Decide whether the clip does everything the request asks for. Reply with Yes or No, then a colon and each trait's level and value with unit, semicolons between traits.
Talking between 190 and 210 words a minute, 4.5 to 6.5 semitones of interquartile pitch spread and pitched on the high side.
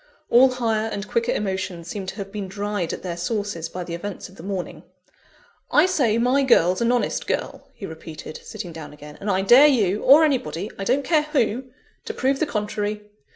Yes: average, 200 wpm; average, 4.9 semitones; high, 205 Hz